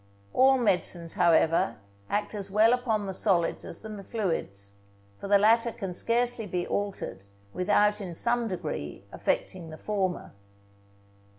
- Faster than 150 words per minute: No, slow, 135 wpm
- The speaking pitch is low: No, high, 200 Hz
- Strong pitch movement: No, average, 4.2 semitones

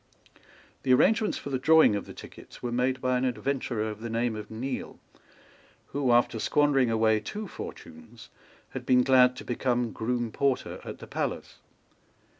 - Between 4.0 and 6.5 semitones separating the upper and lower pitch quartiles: No, average, 2.7 semitones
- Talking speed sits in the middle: Yes, average, 165 wpm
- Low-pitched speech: Yes, low, 125 Hz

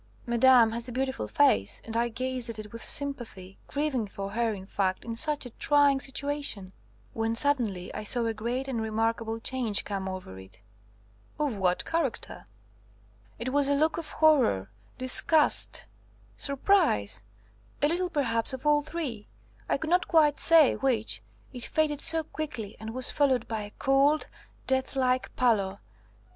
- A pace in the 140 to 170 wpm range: Yes, average, 155 wpm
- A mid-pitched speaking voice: No, very high, 250 Hz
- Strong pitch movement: No, average, 4.6 semitones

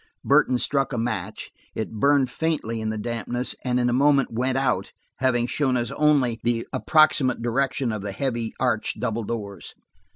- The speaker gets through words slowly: No, average, 170 wpm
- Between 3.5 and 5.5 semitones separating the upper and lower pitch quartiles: No, average, 2.8 semitones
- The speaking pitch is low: Yes, low, 125 Hz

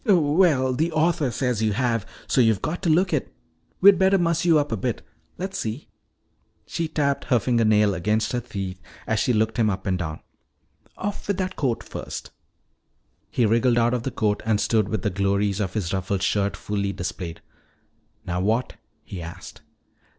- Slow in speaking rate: No, average, 180 wpm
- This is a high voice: No, low, 115 Hz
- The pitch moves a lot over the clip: Yes, wide, 7.0 semitones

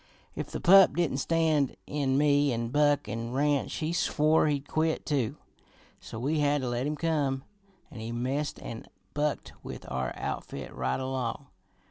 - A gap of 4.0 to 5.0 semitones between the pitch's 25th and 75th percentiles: No, average, 3.1 semitones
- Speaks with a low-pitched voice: No, medium, 145 Hz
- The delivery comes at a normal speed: Yes, average, 165 wpm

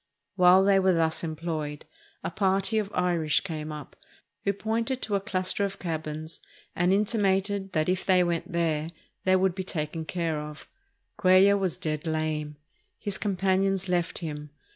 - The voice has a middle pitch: Yes, medium, 180 Hz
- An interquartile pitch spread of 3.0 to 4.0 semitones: Yes, average, 3.6 semitones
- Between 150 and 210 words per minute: Yes, average, 160 wpm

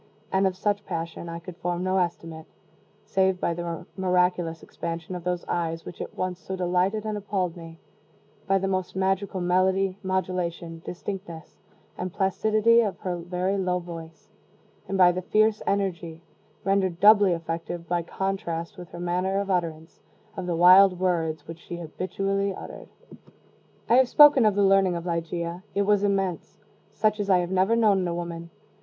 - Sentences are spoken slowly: No, average, 170 wpm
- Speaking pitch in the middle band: Yes, medium, 180 Hz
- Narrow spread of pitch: Yes, narrow, 2.3 semitones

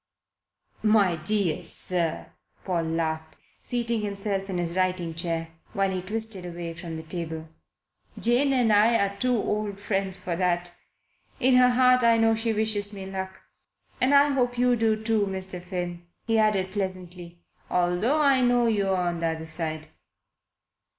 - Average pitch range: Yes, average, 4.3 semitones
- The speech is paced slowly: No, average, 155 wpm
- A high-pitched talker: Yes, high, 195 Hz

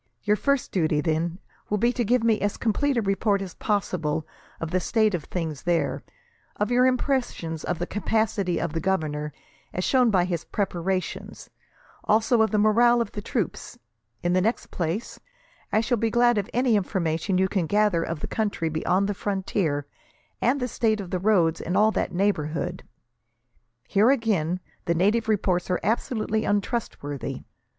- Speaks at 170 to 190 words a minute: Yes, average, 175 wpm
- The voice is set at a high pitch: Yes, high, 200 Hz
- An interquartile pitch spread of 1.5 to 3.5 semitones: No, average, 4.3 semitones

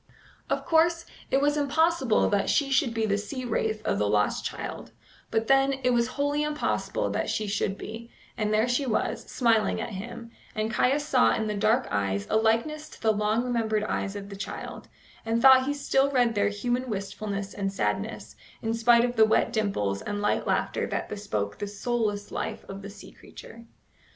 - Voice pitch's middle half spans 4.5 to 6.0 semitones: No, average, 3.9 semitones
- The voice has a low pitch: No, high, 225 Hz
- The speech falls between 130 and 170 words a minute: No, average, 195 wpm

